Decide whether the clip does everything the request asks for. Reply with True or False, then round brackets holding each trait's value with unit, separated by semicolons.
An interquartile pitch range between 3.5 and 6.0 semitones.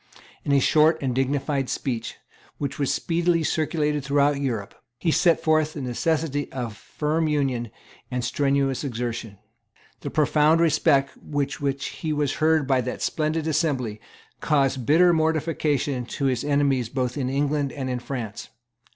False (3.0 semitones)